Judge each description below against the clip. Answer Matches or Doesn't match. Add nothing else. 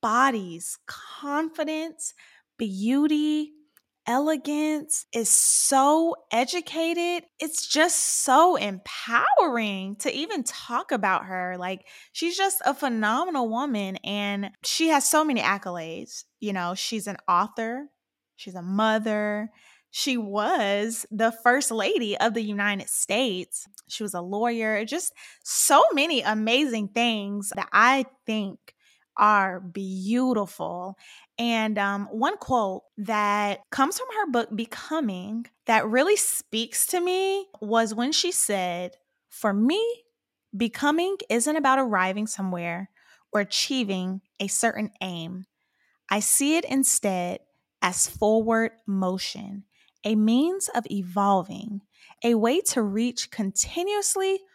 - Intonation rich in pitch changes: Matches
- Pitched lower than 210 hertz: Doesn't match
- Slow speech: Matches